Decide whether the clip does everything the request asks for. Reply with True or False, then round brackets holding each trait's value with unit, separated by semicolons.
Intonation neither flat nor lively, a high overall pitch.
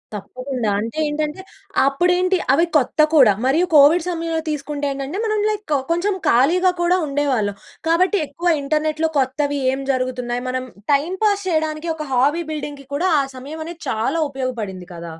True (4.5 semitones; 295 Hz)